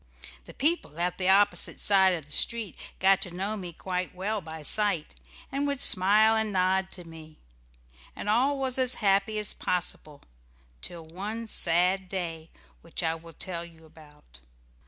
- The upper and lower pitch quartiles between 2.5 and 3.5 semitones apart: No, average, 4.1 semitones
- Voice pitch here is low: No, medium, 185 Hz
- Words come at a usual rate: Yes, average, 165 wpm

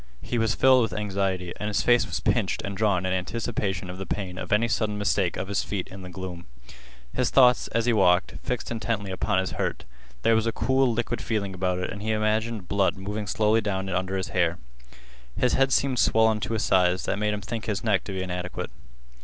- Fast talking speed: Yes, fast, 220 wpm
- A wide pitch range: No, average, 3.2 semitones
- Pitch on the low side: Yes, low, 105 Hz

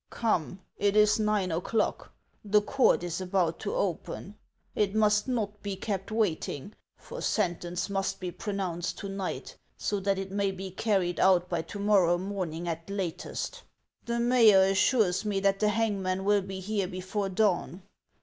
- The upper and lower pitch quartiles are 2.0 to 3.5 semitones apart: Yes, narrow, 2.5 semitones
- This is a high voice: Yes, high, 195 Hz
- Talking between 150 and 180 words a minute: Yes, average, 170 wpm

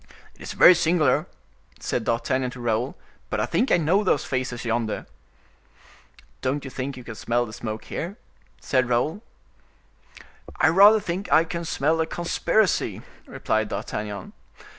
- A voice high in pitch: No, low, 135 Hz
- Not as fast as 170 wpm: Yes, average, 150 wpm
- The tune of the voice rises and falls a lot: Yes, wide, 6.1 semitones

